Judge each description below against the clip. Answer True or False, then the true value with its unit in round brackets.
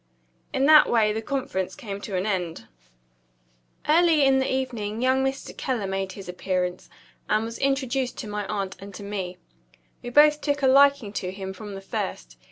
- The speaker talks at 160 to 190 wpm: True (180 wpm)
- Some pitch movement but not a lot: False (5.7 semitones)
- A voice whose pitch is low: False (215 Hz)